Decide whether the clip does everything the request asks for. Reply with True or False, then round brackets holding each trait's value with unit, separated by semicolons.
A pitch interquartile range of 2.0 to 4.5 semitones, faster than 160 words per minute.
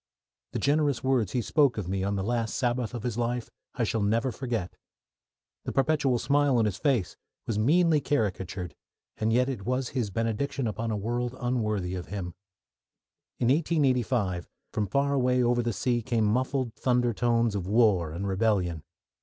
True (3.8 semitones; 170 wpm)